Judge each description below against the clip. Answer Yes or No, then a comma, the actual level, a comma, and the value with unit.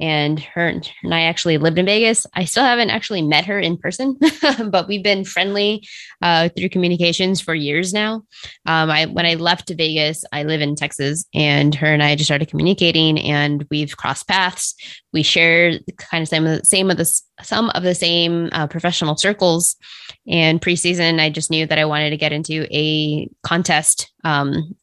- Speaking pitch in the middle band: Yes, medium, 165 Hz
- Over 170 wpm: Yes, average, 180 wpm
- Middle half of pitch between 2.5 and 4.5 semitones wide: Yes, average, 3.2 semitones